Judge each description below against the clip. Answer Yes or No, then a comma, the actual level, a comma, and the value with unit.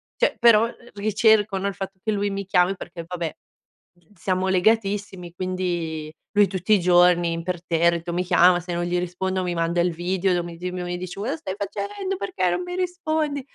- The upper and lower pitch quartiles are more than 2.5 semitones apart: Yes, average, 2.9 semitones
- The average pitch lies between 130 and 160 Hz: No, medium, 185 Hz